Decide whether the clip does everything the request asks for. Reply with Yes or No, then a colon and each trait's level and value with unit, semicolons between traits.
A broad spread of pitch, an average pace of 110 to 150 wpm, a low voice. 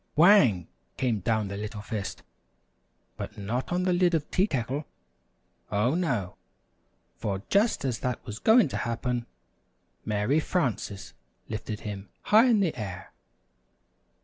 Yes: wide, 8.4 semitones; slow, 135 wpm; low, 120 Hz